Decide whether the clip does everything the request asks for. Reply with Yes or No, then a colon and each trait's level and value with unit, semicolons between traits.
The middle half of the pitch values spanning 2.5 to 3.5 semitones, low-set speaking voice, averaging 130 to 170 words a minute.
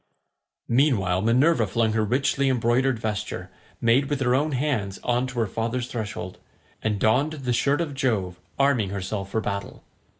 No: average, 4.1 semitones; low, 120 Hz; average, 160 wpm